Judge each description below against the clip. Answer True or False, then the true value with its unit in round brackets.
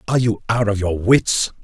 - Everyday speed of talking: False (220 wpm)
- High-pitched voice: False (105 Hz)